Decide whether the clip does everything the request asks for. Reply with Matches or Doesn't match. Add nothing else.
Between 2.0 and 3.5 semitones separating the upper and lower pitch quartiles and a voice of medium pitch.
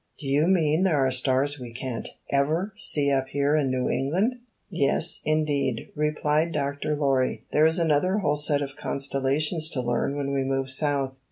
Matches